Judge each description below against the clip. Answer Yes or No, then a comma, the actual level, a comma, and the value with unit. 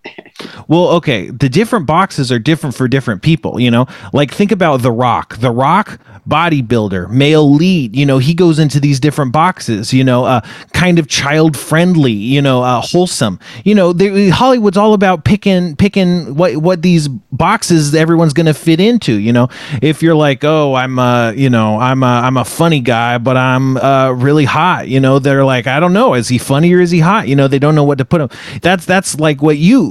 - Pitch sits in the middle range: Yes, medium, 150 Hz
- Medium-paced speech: No, fast, 220 wpm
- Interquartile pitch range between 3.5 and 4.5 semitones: No, average, 5.2 semitones